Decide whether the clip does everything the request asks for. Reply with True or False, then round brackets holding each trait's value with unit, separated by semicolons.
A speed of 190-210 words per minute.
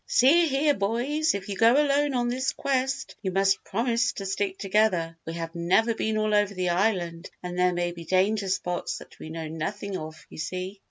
True (205 wpm)